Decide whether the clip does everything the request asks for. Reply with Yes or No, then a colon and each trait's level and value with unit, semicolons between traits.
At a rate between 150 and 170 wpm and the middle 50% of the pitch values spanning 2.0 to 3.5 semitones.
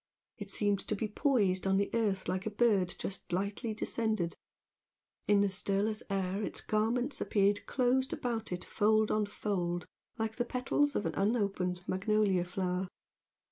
Yes: average, 155 wpm; narrow, 2.6 semitones